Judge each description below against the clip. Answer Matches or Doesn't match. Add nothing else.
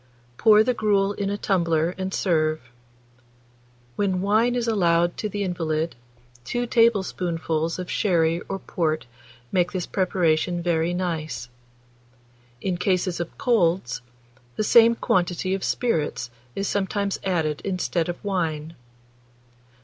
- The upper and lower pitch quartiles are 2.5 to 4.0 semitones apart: Matches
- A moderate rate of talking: Doesn't match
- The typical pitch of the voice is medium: Matches